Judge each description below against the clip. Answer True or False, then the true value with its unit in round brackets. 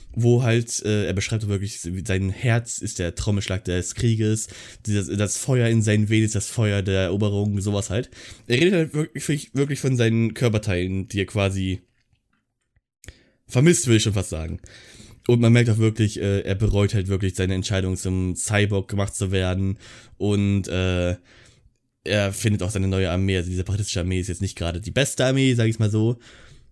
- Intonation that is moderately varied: True (3.2 semitones)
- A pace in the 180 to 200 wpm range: True (185 wpm)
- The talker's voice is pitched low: True (105 Hz)